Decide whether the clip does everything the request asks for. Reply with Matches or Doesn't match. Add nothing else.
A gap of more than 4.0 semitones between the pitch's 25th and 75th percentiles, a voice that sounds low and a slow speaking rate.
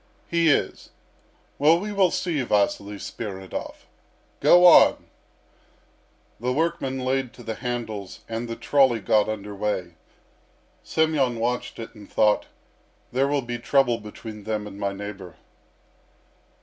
Matches